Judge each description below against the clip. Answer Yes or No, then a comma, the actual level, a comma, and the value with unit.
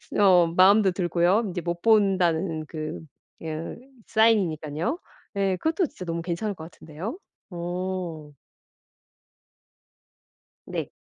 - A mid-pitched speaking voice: Yes, medium, 180 Hz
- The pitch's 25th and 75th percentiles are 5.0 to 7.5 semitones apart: No, average, 3.2 semitones